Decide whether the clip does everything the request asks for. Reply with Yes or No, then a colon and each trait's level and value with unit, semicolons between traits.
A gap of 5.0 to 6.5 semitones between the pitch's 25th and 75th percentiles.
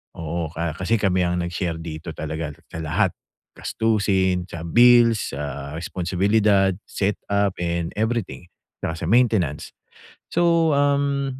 Yes: average, 5.3 semitones